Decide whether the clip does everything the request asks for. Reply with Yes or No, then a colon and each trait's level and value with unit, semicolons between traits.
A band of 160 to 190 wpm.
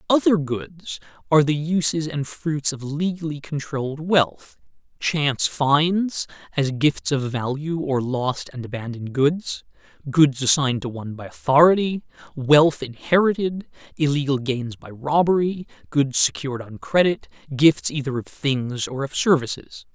No: slow, 135 wpm